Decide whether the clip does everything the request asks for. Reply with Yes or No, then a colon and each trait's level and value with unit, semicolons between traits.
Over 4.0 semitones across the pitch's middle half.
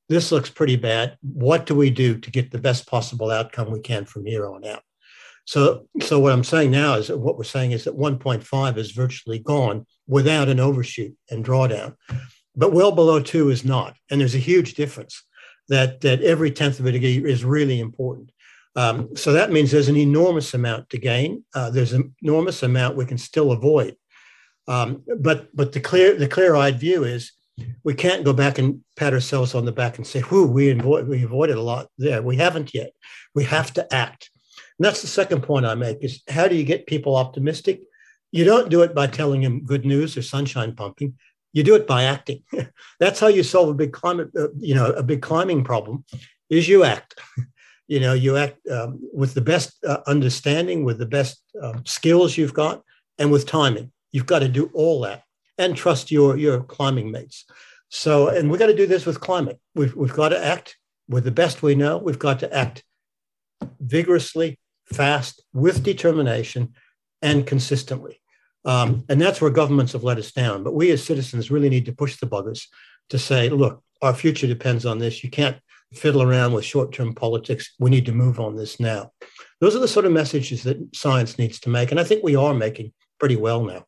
No: average, 3.4 semitones